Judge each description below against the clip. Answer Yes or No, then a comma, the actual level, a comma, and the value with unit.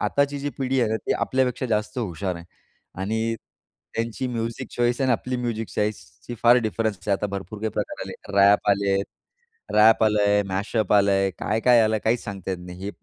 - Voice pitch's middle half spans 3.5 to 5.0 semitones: No, average, 3.0 semitones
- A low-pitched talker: Yes, low, 110 Hz